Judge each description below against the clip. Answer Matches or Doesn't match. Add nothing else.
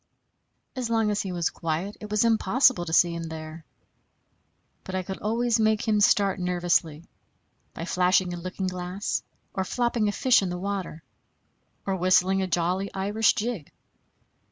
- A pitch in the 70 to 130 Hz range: Doesn't match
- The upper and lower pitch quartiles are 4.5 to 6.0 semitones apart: Doesn't match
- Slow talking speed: Doesn't match